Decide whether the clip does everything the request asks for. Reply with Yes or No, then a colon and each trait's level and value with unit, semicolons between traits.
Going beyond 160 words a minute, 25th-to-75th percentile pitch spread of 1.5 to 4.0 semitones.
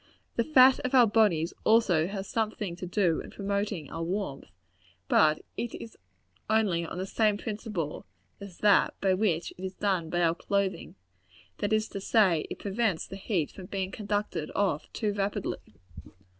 Yes: average, 170 wpm; average, 3.5 semitones